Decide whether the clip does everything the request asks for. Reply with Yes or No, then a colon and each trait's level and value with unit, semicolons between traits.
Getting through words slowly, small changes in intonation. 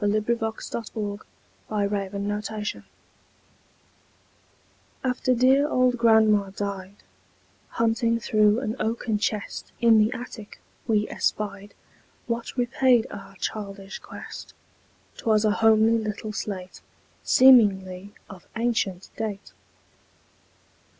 Yes: slow, 95 wpm; narrow, 2.3 semitones